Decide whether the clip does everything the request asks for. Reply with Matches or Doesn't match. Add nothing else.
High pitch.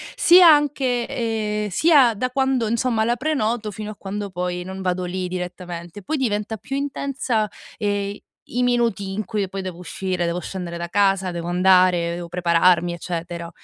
Matches